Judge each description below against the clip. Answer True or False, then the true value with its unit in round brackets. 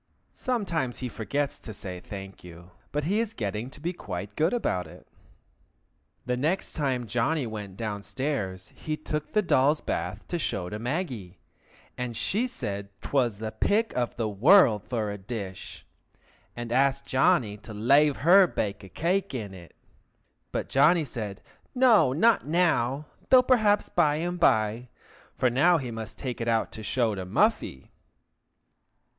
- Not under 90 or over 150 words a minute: False (160 wpm)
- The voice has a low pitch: True (125 Hz)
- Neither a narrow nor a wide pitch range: False (7.3 semitones)